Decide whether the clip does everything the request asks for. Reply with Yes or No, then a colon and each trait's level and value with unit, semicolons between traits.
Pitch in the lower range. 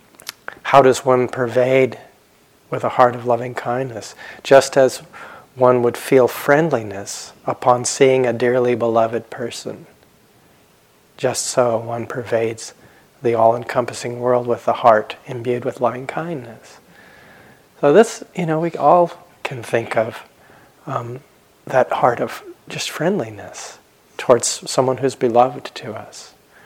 Yes: low, 125 Hz